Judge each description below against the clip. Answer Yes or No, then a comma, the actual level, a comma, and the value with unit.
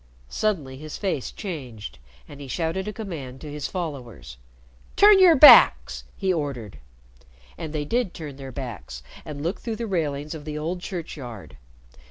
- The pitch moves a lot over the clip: Yes, wide, 5.8 semitones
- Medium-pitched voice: Yes, medium, 150 Hz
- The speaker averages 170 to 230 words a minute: No, average, 160 wpm